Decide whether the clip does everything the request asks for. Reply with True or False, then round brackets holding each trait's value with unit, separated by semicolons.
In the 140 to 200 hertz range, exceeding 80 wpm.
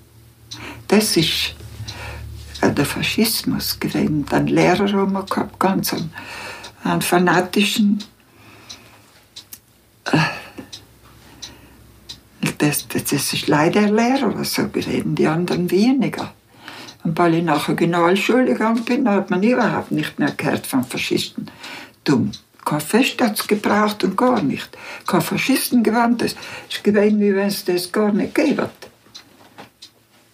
True (185 Hz; 125 wpm)